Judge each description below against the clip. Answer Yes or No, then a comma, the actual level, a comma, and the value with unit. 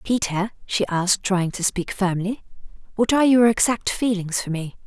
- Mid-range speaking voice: No, high, 200 Hz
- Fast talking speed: No, average, 175 wpm